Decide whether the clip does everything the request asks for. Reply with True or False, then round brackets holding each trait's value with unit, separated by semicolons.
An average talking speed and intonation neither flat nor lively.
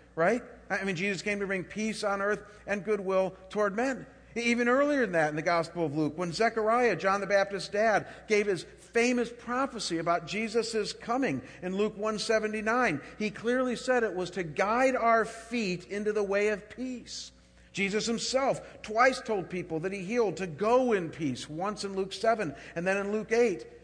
True (185 wpm; 3.3 semitones)